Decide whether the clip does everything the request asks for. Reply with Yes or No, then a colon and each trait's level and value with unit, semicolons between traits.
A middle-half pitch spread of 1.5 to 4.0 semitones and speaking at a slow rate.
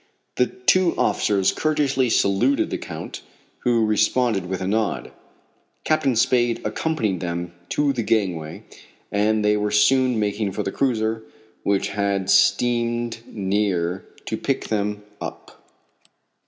Yes: average, 3.5 semitones; slow, 125 wpm